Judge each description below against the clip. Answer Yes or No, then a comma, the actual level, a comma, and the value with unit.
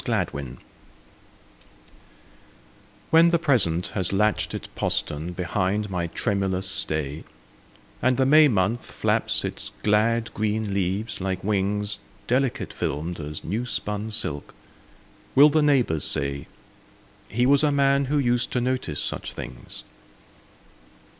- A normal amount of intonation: No, wide, 5.8 semitones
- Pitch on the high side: No, low, 105 Hz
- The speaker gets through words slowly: Yes, slow, 120 wpm